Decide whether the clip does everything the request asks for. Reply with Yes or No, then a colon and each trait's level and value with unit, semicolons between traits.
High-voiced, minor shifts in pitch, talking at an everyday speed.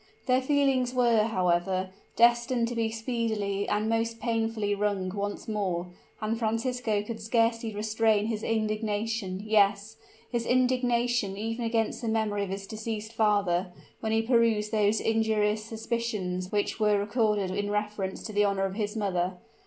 Yes: high, 220 Hz; narrow, 2.0 semitones; average, 150 wpm